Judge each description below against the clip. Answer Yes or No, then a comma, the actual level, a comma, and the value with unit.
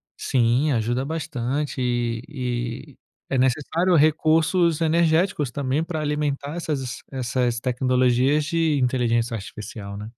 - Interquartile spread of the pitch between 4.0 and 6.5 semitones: Yes, average, 4.3 semitones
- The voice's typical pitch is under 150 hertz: Yes, low, 135 Hz